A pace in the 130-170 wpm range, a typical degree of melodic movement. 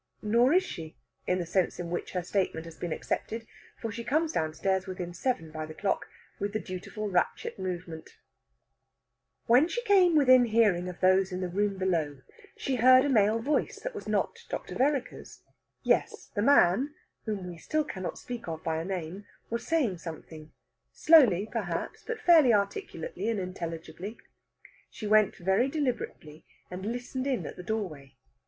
No: average, 165 wpm; wide, 6.2 semitones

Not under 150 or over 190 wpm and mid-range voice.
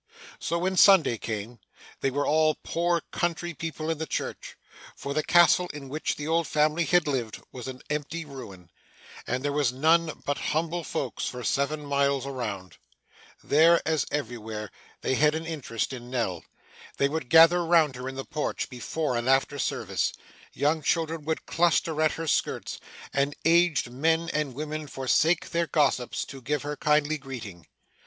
Yes: average, 170 wpm; medium, 150 Hz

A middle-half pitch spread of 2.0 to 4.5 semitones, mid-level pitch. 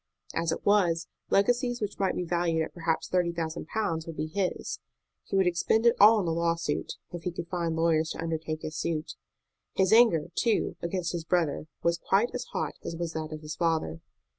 Yes: average, 2.9 semitones; medium, 170 Hz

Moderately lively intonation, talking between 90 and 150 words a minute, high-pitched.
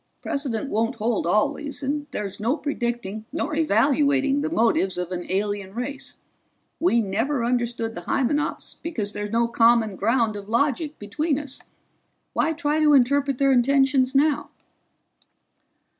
Yes: average, 4.7 semitones; average, 140 wpm; high, 245 Hz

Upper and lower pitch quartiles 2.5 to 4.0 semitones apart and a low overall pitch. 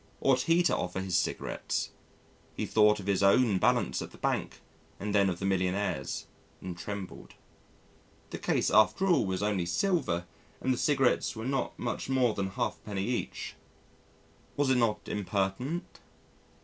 No: average, 5.0 semitones; low, 105 Hz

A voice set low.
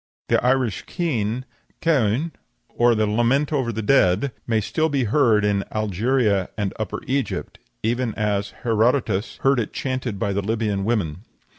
Yes: low, 115 Hz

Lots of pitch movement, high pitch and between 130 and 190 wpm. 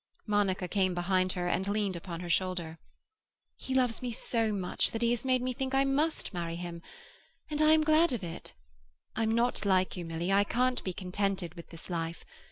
No: wide, 5.7 semitones; high, 195 Hz; average, 200 wpm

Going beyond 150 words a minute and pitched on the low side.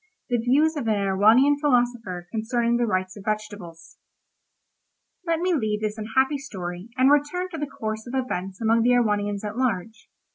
No: average, 170 wpm; high, 225 Hz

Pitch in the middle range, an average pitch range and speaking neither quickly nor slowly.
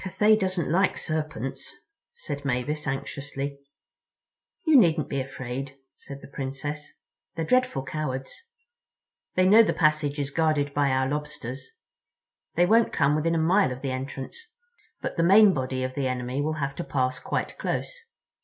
Yes: medium, 145 Hz; average, 3.8 semitones; average, 155 wpm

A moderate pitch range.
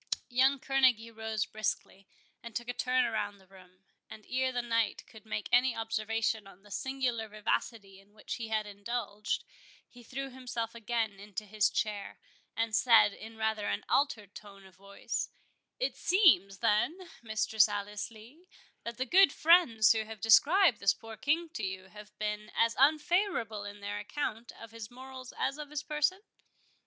Yes: average, 3.7 semitones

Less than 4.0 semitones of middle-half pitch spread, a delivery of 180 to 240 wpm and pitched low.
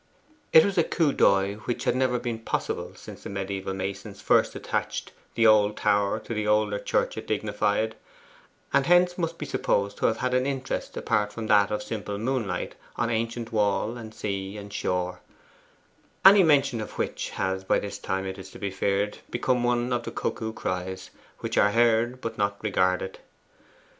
Yes: average, 3.4 semitones; average, 185 wpm; low, 110 Hz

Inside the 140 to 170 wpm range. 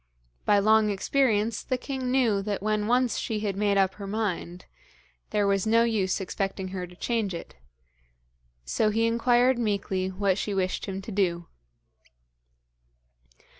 Yes: average, 150 wpm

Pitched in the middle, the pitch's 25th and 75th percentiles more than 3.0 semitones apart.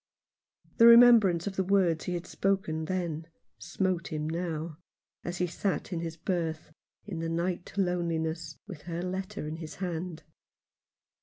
No: medium, 175 Hz; narrow, 2.4 semitones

